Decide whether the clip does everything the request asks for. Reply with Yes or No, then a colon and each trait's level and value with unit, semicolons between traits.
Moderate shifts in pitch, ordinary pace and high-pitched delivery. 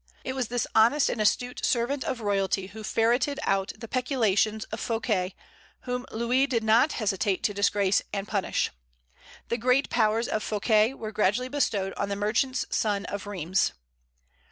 Yes: average, 3.5 semitones; average, 160 wpm; high, 220 Hz